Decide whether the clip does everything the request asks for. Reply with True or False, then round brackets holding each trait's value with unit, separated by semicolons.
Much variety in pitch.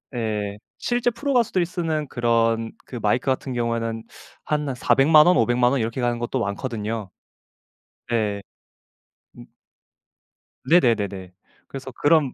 False (4.8 semitones)